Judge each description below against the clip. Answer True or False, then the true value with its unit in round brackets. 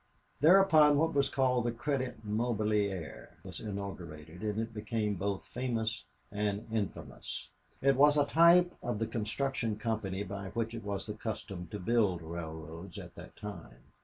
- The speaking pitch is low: True (110 Hz)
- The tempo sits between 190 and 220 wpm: False (155 wpm)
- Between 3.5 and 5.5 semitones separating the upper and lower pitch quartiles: True (4.0 semitones)